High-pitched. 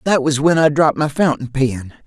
No: medium, 145 Hz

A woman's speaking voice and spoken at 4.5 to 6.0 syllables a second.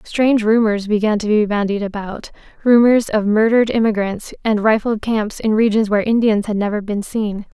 Yes: female; 5.3 syllables/s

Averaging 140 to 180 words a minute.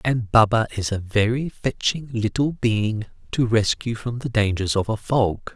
Yes: average, 175 wpm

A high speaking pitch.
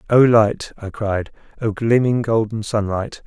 No: low, 110 Hz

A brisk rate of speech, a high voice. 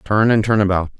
No: fast, 240 wpm; low, 105 Hz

